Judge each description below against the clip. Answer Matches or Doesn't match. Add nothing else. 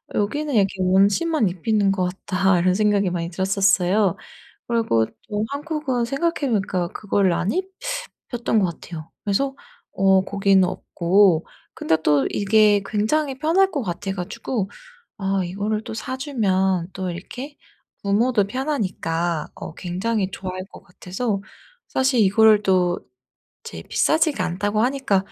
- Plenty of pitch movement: Doesn't match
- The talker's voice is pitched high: Matches